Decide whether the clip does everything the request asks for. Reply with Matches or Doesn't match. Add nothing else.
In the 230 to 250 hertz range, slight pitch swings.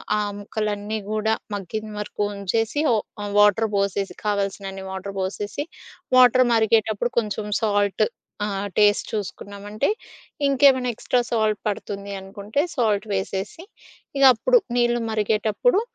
Doesn't match